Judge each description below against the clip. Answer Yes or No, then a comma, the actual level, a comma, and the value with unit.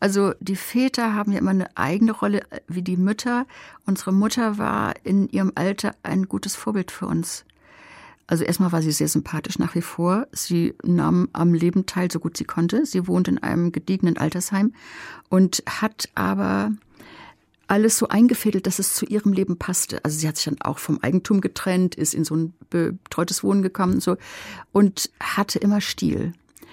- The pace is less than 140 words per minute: No, average, 180 wpm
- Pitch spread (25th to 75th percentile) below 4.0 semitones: Yes, average, 3.3 semitones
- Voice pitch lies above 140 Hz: Yes, medium, 185 Hz